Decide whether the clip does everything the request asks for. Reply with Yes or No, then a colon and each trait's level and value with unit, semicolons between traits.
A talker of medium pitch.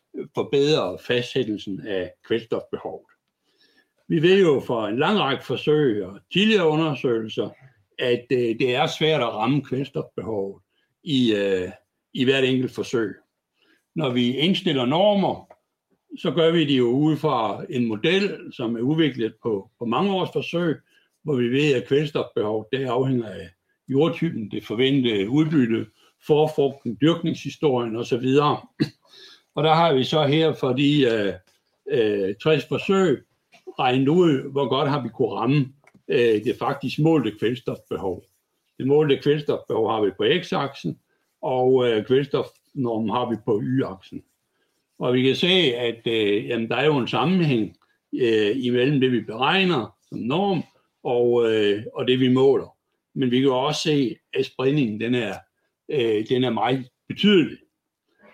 No: low, 130 Hz